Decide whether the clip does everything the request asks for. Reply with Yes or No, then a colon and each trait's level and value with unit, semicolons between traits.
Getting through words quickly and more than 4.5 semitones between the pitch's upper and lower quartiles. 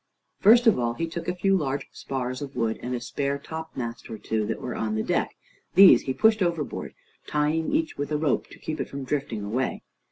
Yes: fast, 220 wpm; average, 5.1 semitones